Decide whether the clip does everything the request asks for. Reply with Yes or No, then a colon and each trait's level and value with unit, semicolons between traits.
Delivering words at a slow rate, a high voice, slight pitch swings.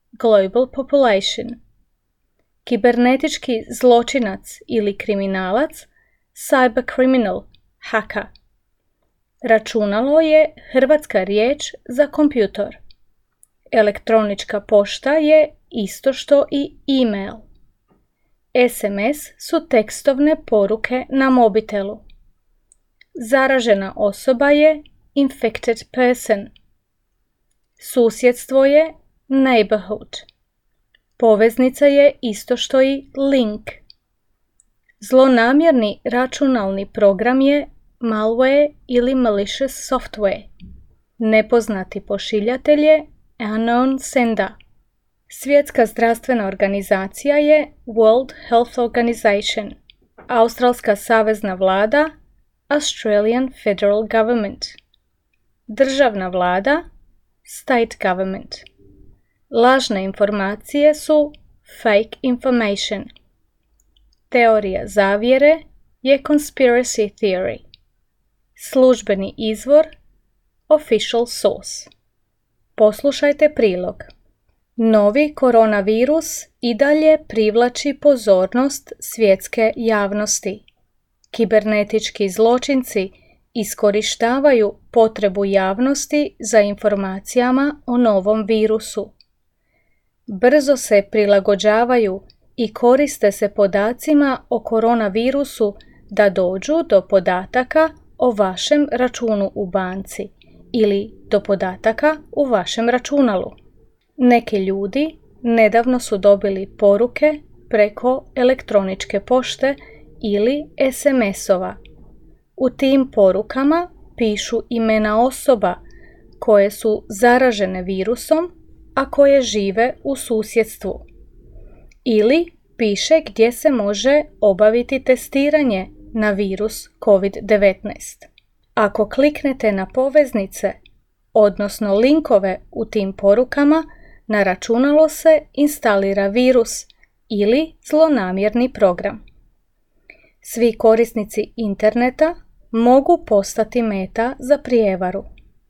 No: slow, 80 wpm; high, 230 Hz; average, 4.6 semitones